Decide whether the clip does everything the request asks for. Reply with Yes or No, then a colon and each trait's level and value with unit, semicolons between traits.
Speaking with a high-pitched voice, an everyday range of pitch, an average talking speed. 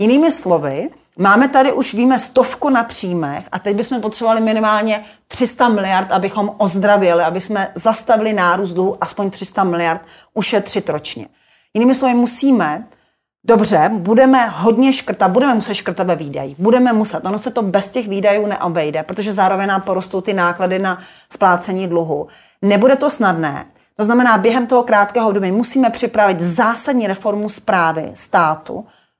Yes: high, 210 Hz; average, 3.8 semitones; average, 150 wpm